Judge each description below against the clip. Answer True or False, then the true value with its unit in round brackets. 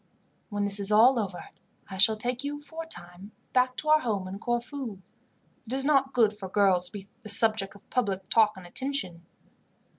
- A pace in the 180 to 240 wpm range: True (200 wpm)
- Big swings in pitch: False (4.6 semitones)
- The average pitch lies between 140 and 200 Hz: False (215 Hz)